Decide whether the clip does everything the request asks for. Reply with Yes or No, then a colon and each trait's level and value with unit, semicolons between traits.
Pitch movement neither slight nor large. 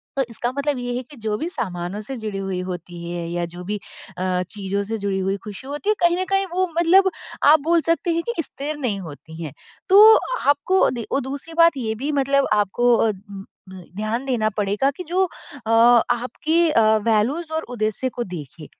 No: wide, 7.6 semitones